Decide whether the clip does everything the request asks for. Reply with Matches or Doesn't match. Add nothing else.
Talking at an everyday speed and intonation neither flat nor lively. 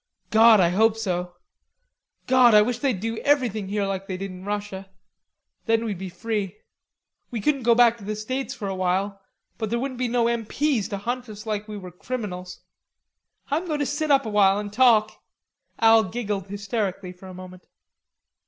Matches